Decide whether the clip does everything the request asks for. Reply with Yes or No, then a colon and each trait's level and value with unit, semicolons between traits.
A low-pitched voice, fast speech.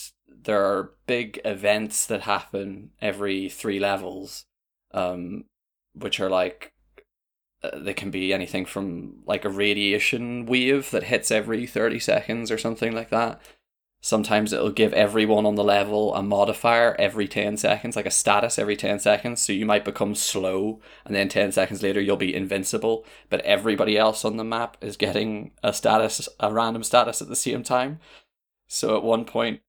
No: low, 105 Hz; average, 170 wpm